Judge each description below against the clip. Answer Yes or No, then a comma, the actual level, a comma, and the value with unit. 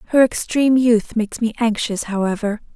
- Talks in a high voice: Yes, high, 225 Hz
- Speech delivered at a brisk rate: No, average, 155 wpm